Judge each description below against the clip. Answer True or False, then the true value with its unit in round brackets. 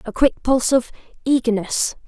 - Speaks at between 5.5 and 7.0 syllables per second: False (5.2 syllables/s)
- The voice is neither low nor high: False (245 Hz)